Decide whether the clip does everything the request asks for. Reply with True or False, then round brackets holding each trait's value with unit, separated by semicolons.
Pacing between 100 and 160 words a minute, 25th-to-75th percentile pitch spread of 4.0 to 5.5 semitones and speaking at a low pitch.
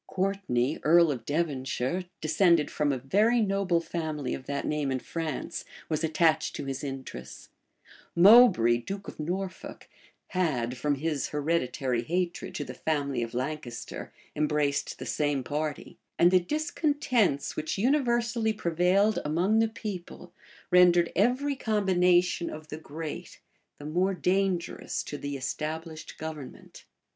False (135 wpm; 4.8 semitones; 160 Hz)